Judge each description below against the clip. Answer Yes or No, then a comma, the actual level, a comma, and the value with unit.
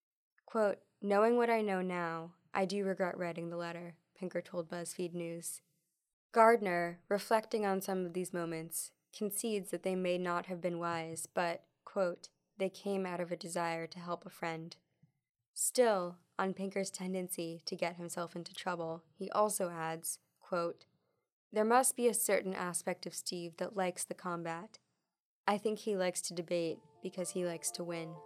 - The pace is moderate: Yes, average, 170 wpm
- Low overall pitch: No, medium, 180 Hz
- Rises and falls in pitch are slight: Yes, narrow, 2.2 semitones